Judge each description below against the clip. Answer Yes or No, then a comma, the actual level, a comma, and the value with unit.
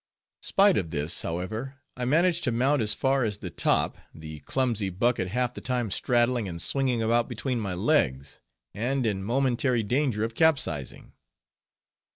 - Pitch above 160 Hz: No, low, 120 Hz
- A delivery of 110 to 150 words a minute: No, average, 160 wpm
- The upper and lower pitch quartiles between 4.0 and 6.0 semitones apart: Yes, average, 5.1 semitones